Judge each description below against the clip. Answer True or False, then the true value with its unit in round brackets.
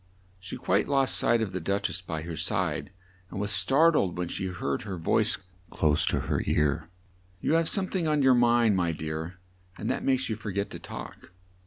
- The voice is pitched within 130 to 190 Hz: False (95 Hz)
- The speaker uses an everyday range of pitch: False (6.5 semitones)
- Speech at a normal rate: False (210 wpm)